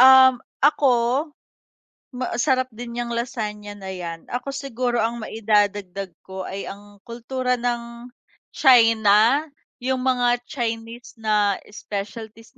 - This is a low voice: No, high, 235 Hz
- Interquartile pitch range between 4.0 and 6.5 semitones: No, average, 3.3 semitones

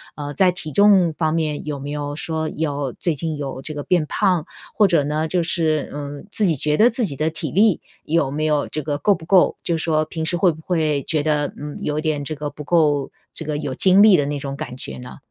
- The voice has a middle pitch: Yes, medium, 155 Hz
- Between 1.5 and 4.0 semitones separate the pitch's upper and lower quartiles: Yes, narrow, 2.6 semitones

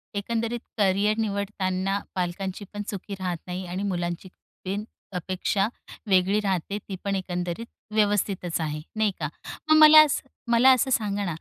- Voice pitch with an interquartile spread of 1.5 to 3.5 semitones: Yes, narrow, 2.5 semitones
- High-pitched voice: Yes, high, 195 Hz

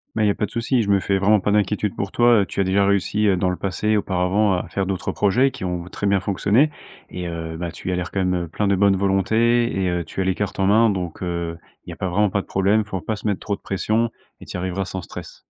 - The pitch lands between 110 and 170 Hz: No, low, 100 Hz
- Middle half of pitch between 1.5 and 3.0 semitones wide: Yes, narrow, 2.4 semitones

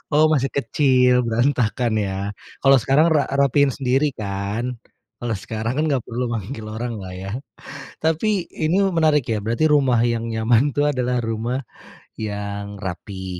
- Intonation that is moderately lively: Yes, average, 4.4 semitones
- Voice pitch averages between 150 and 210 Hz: No, low, 120 Hz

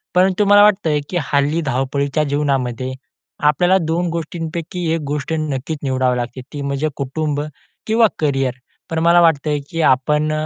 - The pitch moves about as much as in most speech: Yes, average, 3.2 semitones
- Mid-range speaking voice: Yes, medium, 150 Hz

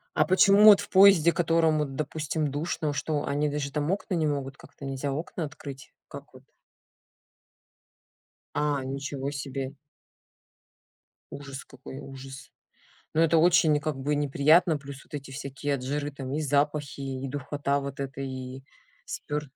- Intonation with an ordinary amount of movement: No, narrow, 2.2 semitones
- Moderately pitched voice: Yes, medium, 145 Hz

